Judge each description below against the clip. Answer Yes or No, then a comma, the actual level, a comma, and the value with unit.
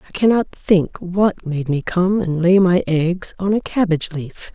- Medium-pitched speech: Yes, medium, 180 Hz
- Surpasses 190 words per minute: Yes, average, 200 wpm